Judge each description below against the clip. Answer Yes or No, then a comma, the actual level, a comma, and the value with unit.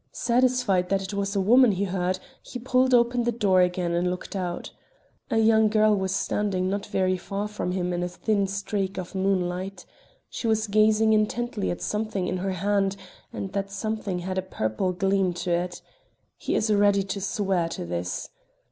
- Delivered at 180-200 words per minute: Yes, average, 185 wpm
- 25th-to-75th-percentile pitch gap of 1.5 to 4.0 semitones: Yes, average, 2.7 semitones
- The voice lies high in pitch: Yes, high, 195 Hz